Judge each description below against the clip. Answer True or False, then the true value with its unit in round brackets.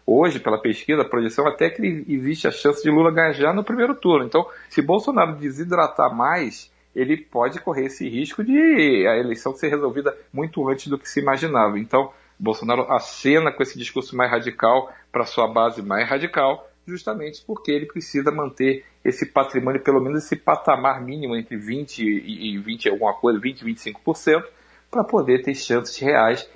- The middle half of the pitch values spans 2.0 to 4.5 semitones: True (4.2 semitones)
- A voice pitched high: False (135 Hz)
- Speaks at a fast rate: False (170 wpm)